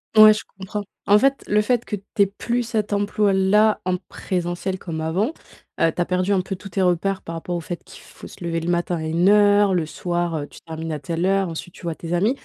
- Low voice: No, medium, 185 Hz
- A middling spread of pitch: Yes, average, 3.1 semitones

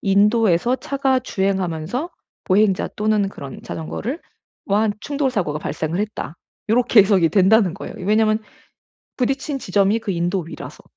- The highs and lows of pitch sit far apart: No, average, 4.1 semitones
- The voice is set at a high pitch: Yes, high, 205 Hz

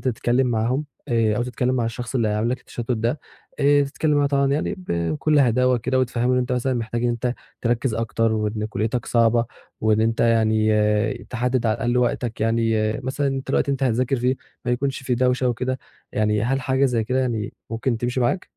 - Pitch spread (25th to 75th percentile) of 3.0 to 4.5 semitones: No, narrow, 2.4 semitones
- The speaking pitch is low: Yes, low, 120 Hz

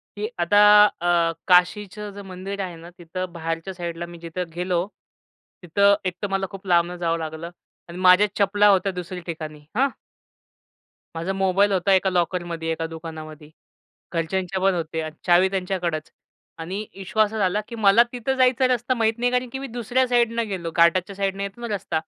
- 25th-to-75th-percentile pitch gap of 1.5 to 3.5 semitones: Yes, average, 3.2 semitones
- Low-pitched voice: No, medium, 185 Hz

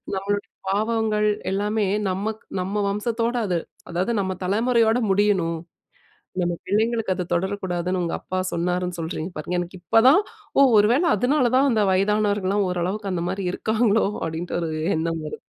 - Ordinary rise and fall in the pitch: Yes, average, 3.4 semitones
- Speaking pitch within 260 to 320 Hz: No, high, 200 Hz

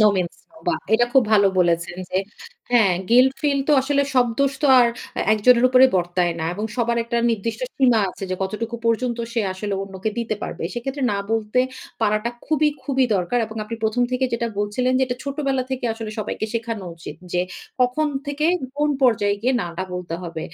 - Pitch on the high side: Yes, high, 230 Hz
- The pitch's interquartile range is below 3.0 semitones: No, average, 4.0 semitones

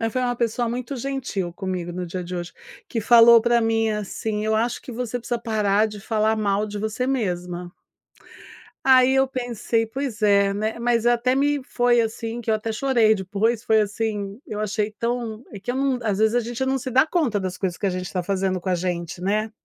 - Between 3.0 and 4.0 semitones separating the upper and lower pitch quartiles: Yes, average, 3.3 semitones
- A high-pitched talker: Yes, high, 220 Hz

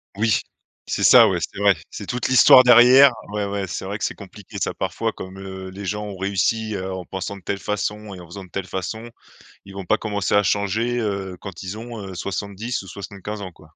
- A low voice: Yes, low, 100 Hz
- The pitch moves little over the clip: Yes, narrow, 2.0 semitones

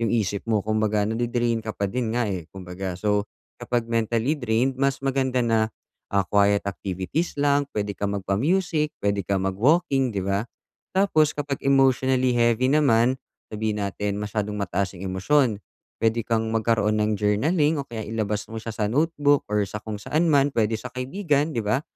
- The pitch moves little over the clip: No, average, 4.5 semitones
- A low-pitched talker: Yes, low, 115 Hz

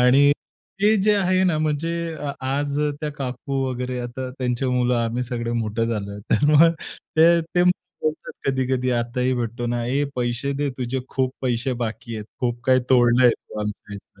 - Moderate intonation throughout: Yes, average, 3.0 semitones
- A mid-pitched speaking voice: No, low, 125 Hz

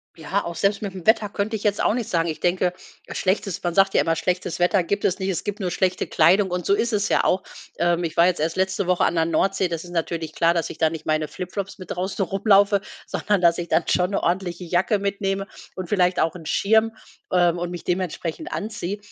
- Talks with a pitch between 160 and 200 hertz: Yes, medium, 185 Hz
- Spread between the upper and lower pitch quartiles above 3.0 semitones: No, narrow, 2.6 semitones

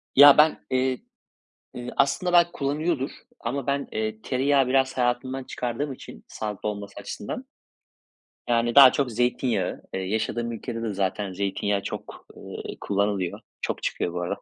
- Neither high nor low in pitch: No, low, 120 Hz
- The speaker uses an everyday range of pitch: Yes, average, 4.8 semitones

